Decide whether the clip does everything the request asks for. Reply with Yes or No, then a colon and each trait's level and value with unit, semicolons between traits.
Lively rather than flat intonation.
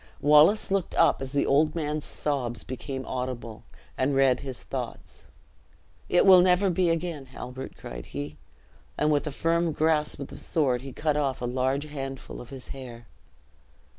No: average, 3.4 semitones